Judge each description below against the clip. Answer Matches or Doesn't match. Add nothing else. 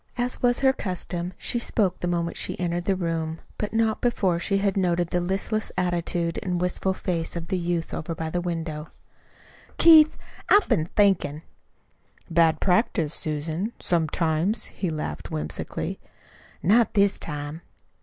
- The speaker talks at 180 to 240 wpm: Doesn't match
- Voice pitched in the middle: Matches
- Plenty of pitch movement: Doesn't match